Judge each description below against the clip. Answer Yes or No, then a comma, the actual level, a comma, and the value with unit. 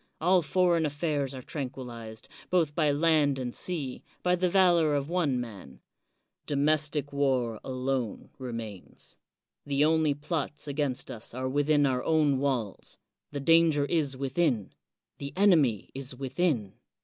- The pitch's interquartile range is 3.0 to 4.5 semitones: Yes, average, 3.6 semitones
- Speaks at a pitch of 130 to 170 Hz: Yes, medium, 140 Hz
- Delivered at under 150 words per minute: Yes, average, 140 wpm